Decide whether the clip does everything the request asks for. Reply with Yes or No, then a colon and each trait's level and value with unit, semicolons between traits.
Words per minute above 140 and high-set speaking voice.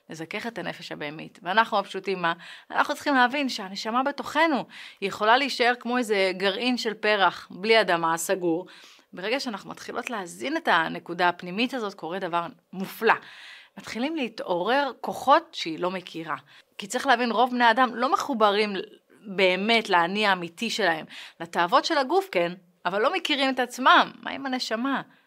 Yes: fast, 150 wpm; high, 220 Hz